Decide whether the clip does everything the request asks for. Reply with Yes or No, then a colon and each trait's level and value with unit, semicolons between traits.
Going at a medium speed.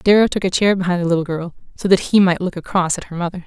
No: fast, 295 wpm